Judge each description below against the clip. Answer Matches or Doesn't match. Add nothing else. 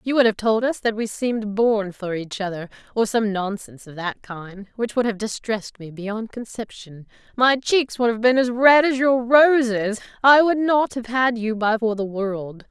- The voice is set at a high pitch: Matches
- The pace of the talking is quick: Matches